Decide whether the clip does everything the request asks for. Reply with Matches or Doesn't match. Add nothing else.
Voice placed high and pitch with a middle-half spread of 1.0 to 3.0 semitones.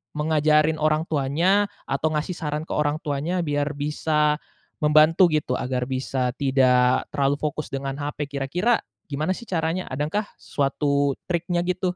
Doesn't match